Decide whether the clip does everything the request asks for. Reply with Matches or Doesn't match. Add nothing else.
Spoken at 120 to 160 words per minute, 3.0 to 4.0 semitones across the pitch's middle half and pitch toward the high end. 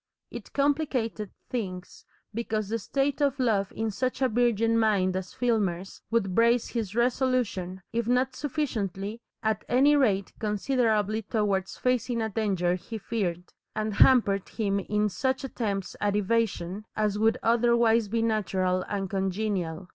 Matches